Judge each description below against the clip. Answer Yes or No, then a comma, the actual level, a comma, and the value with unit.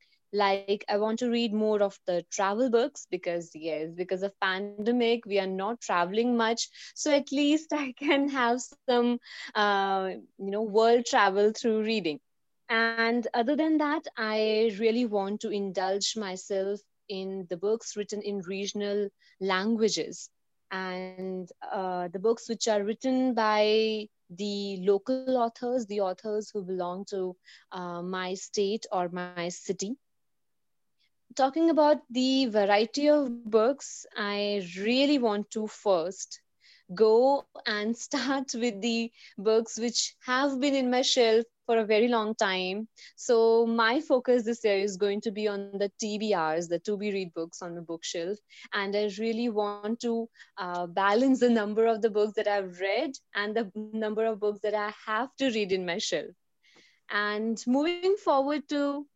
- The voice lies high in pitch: Yes, high, 215 Hz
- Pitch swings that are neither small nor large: Yes, average, 3.3 semitones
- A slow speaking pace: No, average, 155 wpm